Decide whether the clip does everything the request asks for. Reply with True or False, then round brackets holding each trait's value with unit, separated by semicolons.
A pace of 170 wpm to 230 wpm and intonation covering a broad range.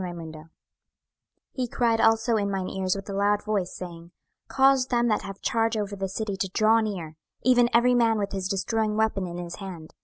False (195 wpm; 3.2 semitones)